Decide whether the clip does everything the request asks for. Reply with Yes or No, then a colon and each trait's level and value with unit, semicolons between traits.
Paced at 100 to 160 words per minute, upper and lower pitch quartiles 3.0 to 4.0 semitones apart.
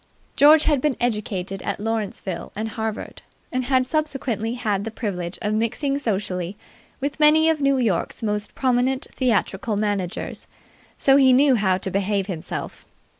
No: average, 150 wpm; average, 4.9 semitones